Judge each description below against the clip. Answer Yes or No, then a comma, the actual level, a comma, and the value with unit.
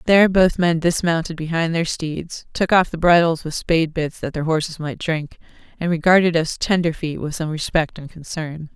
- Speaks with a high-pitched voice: No, medium, 165 Hz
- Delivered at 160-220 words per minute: Yes, average, 190 wpm